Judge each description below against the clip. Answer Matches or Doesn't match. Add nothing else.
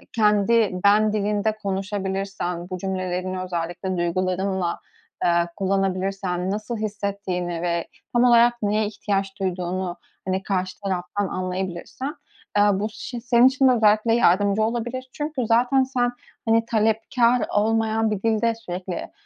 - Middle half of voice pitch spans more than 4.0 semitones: Doesn't match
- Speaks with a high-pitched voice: Matches